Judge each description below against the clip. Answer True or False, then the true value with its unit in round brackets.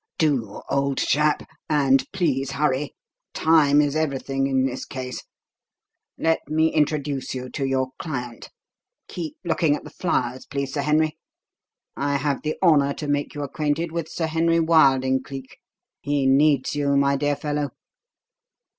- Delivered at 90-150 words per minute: True (145 wpm)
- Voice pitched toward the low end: False (145 Hz)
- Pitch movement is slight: True (2.3 semitones)